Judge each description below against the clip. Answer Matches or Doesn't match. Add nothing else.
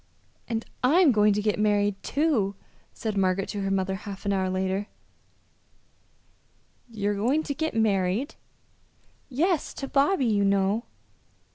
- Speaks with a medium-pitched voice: Doesn't match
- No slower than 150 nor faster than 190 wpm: Doesn't match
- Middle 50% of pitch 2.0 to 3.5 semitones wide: Doesn't match